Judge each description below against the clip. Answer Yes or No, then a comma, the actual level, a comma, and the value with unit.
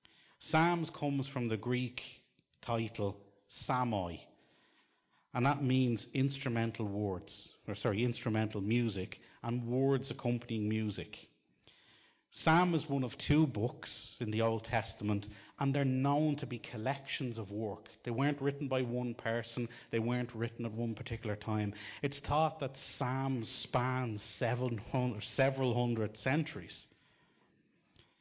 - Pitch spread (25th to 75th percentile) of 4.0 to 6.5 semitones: No, average, 3.5 semitones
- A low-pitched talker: Yes, low, 120 Hz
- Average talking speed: No, slow, 125 wpm